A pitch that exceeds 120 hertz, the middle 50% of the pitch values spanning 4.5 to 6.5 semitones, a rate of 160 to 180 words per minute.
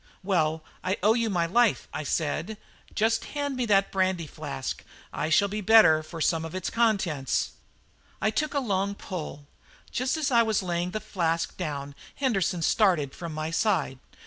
Yes: medium, 185 Hz; average, 5.3 semitones; average, 175 wpm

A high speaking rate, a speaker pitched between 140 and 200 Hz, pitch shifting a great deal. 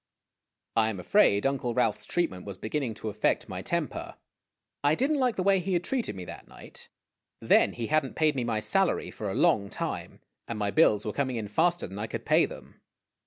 No: fast, 215 wpm; low, 120 Hz; wide, 8.2 semitones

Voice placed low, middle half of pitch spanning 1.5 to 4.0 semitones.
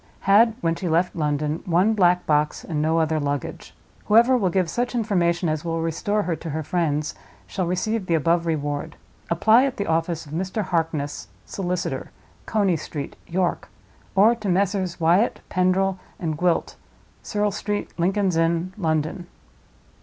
No: medium, 175 Hz; average, 3.5 semitones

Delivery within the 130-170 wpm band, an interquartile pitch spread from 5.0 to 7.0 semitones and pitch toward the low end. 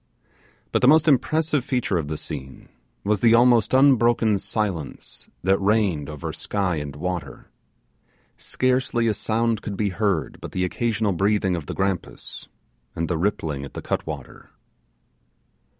Yes: average, 150 wpm; wide, 5.4 semitones; low, 100 Hz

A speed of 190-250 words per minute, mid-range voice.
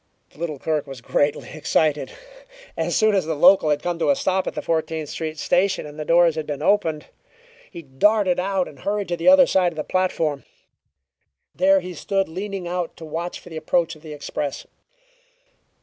Yes: average, 195 wpm; medium, 165 Hz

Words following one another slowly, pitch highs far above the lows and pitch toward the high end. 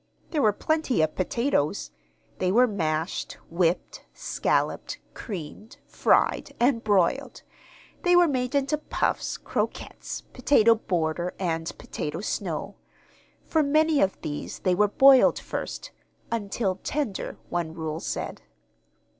Yes: slow, 120 wpm; wide, 7.7 semitones; high, 210 Hz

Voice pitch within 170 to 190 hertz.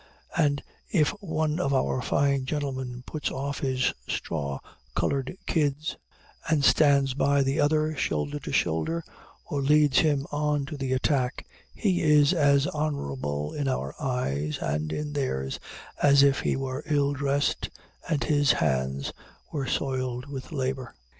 No: medium, 140 Hz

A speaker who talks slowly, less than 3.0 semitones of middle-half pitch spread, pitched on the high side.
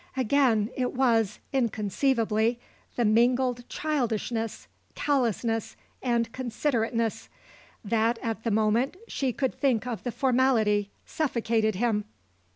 Yes: slow, 105 wpm; narrow, 2.6 semitones; high, 235 Hz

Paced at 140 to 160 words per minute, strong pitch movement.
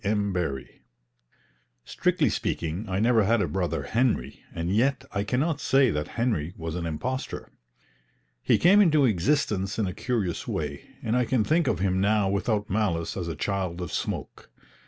No: average, 175 wpm; wide, 5.8 semitones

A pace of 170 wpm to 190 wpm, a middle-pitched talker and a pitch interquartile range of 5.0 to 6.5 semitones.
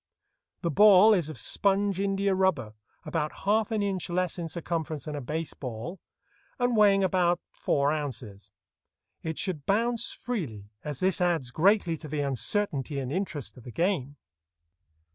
No: average, 155 wpm; medium, 170 Hz; wide, 5.4 semitones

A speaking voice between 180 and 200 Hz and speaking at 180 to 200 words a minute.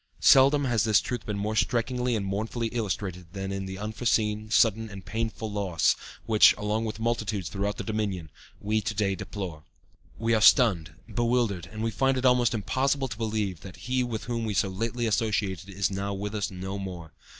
No: low, 105 Hz; average, 190 wpm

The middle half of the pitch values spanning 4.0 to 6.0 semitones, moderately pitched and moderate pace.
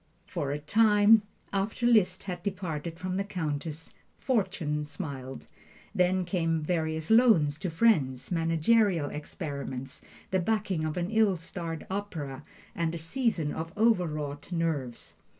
No: average, 4.7 semitones; medium, 165 Hz; slow, 130 wpm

